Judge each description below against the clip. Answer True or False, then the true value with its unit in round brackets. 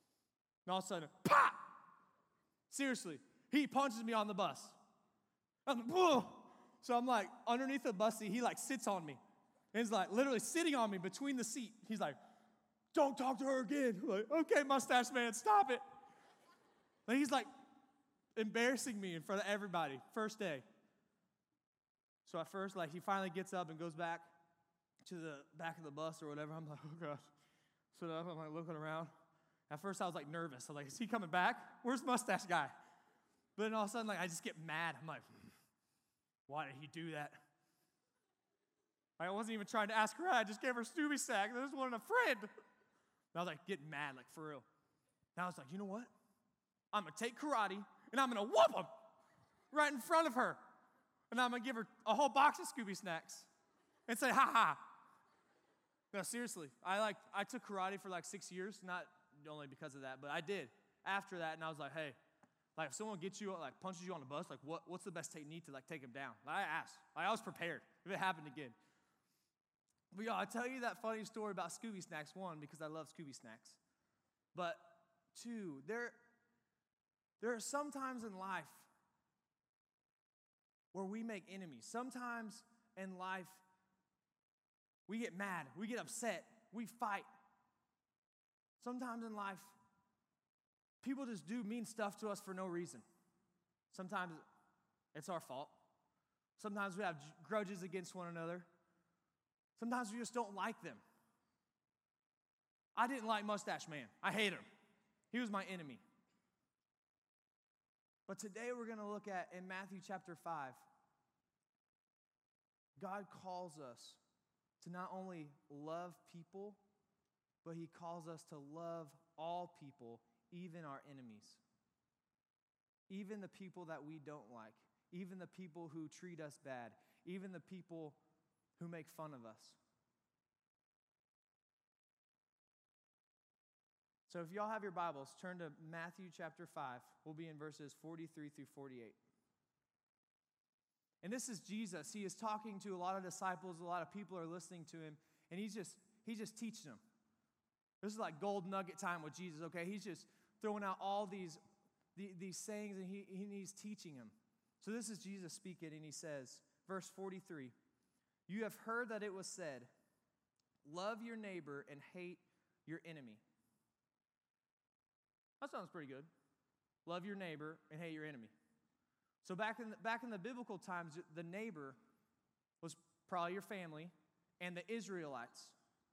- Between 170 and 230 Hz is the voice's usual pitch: True (190 Hz)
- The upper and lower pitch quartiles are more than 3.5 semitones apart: True (5.0 semitones)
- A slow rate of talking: False (170 wpm)